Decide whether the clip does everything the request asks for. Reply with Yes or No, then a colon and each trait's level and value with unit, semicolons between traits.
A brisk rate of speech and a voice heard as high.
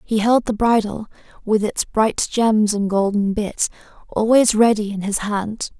No: average, 165 wpm; high, 215 Hz